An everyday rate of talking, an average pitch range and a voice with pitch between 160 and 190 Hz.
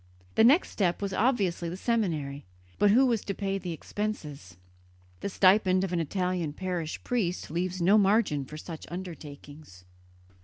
Yes: average, 155 wpm; average, 4.2 semitones; medium, 185 Hz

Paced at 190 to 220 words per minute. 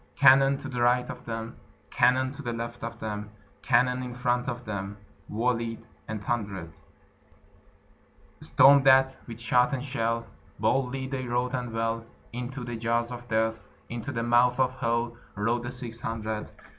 No: average, 160 wpm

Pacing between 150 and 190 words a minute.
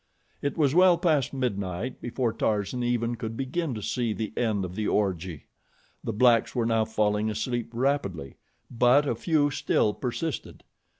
Yes: average, 160 wpm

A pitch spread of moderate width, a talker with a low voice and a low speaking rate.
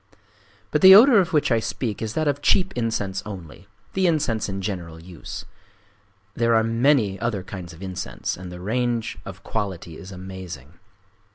No: average, 4.9 semitones; low, 105 Hz; average, 165 wpm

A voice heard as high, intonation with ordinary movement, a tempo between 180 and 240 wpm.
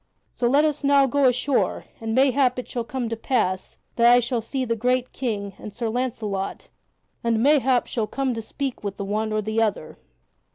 Yes: high, 240 Hz; average, 3.2 semitones; average, 200 wpm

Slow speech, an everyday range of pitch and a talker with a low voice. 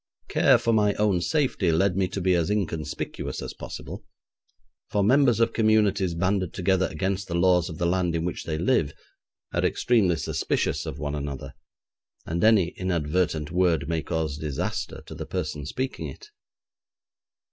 No: average, 160 wpm; average, 3.9 semitones; very low, 90 Hz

